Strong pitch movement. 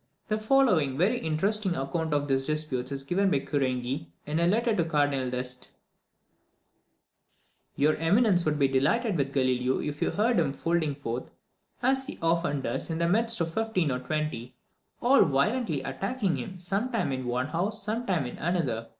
Yes: wide, 6.7 semitones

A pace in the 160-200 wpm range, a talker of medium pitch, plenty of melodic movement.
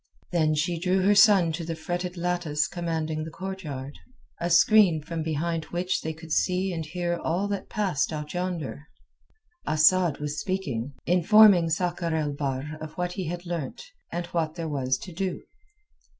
No: average, 165 wpm; medium, 170 Hz; average, 2.7 semitones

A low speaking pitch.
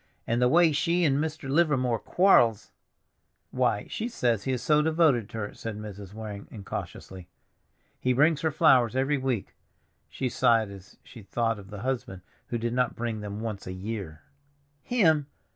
Yes: low, 120 Hz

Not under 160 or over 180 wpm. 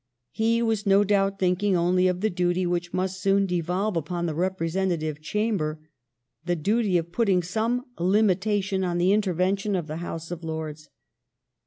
Yes: average, 170 wpm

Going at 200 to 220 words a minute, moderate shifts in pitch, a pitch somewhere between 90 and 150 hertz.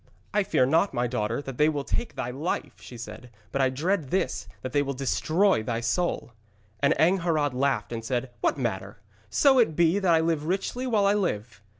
No: fast, 205 wpm; wide, 6.1 semitones; medium, 140 Hz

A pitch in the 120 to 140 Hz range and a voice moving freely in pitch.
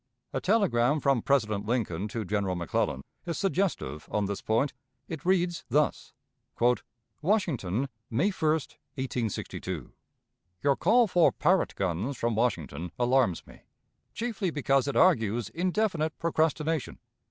Yes: low, 135 Hz; wide, 7.9 semitones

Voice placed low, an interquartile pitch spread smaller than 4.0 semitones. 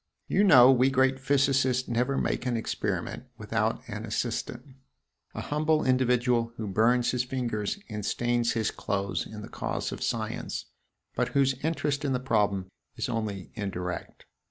Yes: low, 125 Hz; average, 3.5 semitones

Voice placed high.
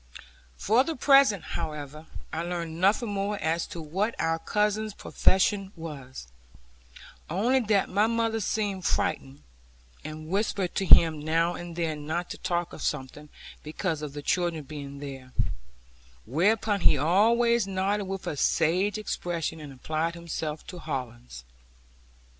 No: medium, 170 Hz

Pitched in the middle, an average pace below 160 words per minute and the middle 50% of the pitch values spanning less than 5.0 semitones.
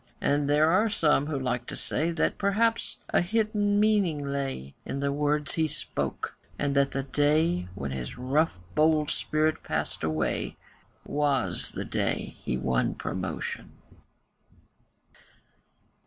Yes: medium, 145 Hz; average, 140 wpm; average, 3.4 semitones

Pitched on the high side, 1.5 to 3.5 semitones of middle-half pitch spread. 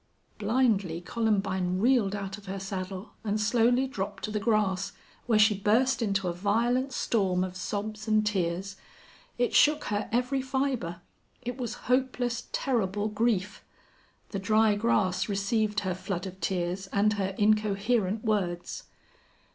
Yes: high, 210 Hz; average, 3.2 semitones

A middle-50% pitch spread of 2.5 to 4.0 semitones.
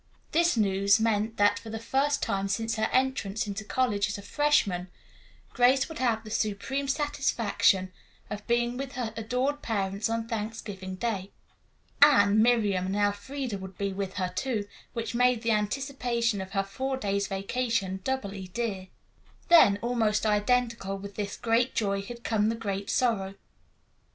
Yes: average, 3.5 semitones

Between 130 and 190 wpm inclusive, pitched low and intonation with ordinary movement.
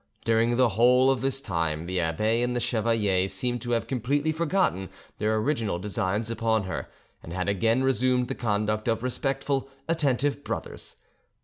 Yes: average, 165 wpm; low, 115 Hz; average, 3.9 semitones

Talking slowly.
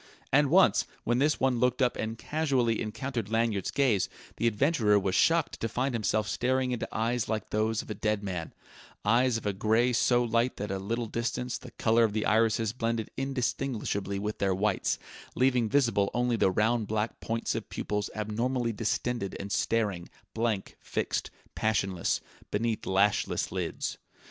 No: average, 170 wpm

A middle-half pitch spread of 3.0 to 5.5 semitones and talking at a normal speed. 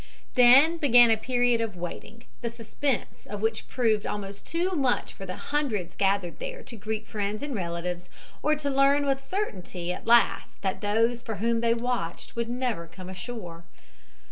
Yes: average, 4.3 semitones; average, 170 wpm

